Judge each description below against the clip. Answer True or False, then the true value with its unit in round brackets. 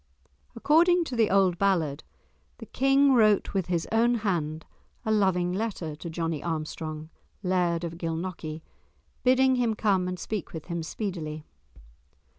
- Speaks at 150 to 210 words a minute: False (140 wpm)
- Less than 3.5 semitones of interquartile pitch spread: False (5.2 semitones)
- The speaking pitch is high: False (180 Hz)